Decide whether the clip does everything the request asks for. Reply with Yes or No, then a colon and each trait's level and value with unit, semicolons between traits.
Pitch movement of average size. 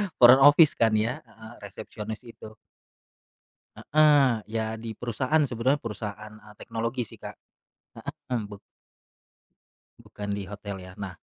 Yes: average, 3.0 semitones